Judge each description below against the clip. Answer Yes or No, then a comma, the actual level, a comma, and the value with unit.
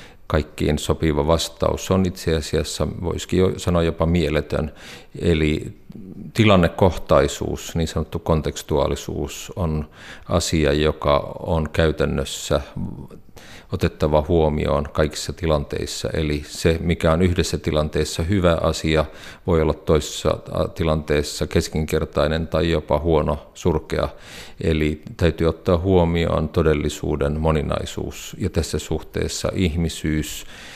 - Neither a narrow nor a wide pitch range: No, narrow, 1.9 semitones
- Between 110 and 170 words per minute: No, average, 100 wpm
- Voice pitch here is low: Yes, very low, 80 Hz